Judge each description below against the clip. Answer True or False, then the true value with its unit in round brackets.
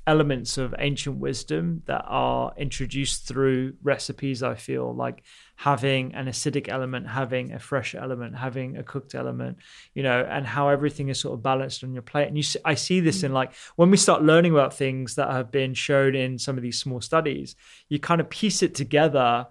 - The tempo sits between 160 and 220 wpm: True (200 wpm)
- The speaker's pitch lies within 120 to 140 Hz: True (135 Hz)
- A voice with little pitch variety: True (2.2 semitones)